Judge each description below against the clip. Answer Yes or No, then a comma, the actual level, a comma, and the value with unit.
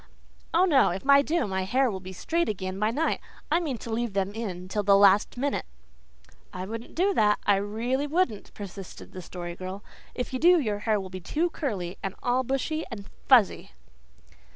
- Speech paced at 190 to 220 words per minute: Yes, average, 200 wpm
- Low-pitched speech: No, high, 215 Hz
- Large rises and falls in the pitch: Yes, wide, 6.0 semitones